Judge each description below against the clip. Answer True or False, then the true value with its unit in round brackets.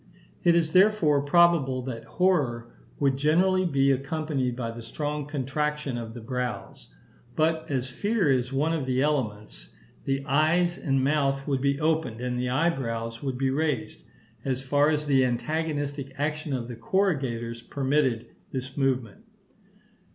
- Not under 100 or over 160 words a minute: True (150 wpm)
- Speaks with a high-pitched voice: False (135 Hz)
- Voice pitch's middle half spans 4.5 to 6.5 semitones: False (3.4 semitones)